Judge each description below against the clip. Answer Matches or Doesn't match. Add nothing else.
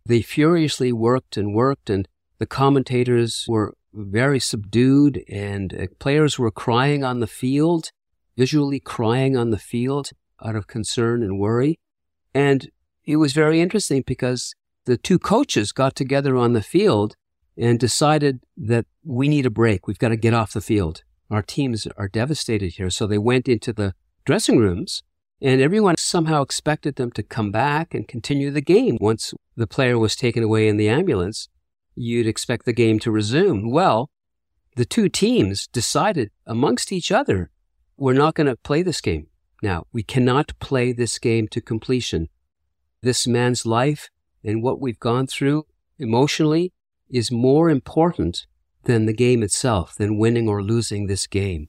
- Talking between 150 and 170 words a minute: Matches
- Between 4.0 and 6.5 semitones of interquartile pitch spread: Matches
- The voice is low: Matches